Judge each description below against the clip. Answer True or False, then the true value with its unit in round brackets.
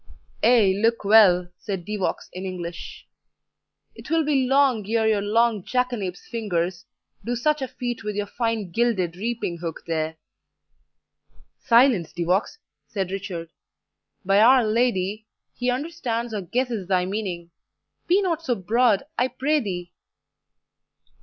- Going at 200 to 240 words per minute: False (140 wpm)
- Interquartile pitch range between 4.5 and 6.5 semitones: True (4.9 semitones)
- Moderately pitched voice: False (215 Hz)